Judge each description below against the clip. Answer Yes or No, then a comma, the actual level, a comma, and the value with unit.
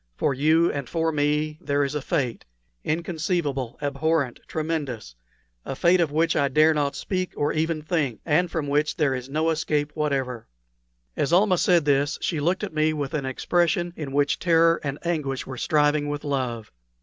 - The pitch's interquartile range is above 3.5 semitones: No, narrow, 2.6 semitones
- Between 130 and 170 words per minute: No, average, 180 wpm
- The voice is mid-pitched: Yes, medium, 150 Hz